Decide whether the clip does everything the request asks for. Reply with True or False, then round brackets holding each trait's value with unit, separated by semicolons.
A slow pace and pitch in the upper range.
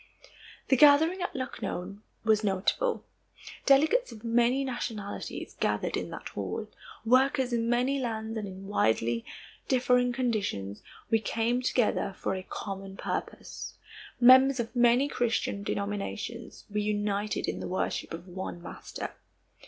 True (130 wpm; 230 Hz)